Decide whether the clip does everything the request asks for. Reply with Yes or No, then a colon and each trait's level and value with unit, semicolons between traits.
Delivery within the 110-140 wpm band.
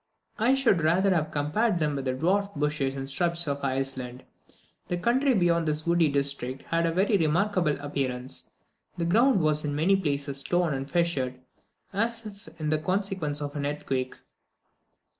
No: average, 160 wpm